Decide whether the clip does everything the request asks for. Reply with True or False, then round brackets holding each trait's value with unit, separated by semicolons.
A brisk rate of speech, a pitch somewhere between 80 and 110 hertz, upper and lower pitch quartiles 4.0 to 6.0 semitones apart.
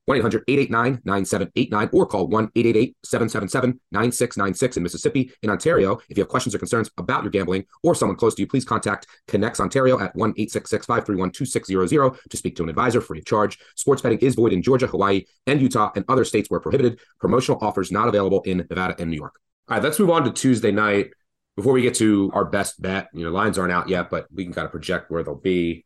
True (225 wpm; 100 Hz; 4.6 semitones)